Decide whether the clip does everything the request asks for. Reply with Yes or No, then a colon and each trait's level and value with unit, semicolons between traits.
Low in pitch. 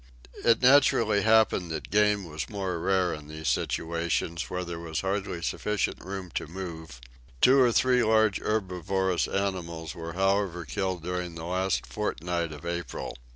Yes: very low, 90 Hz